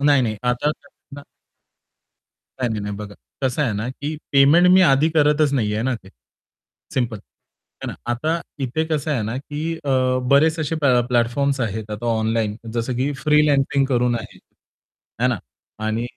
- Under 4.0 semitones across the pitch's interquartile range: No, average, 4.3 semitones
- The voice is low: Yes, low, 130 Hz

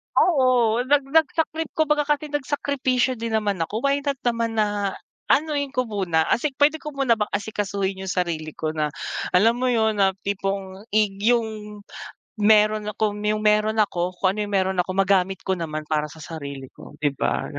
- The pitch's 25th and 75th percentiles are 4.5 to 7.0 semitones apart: Yes, average, 5.2 semitones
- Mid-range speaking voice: No, high, 215 Hz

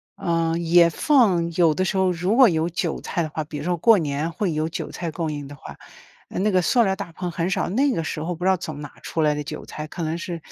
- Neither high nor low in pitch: Yes, medium, 170 Hz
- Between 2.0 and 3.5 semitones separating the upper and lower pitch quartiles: Yes, average, 2.8 semitones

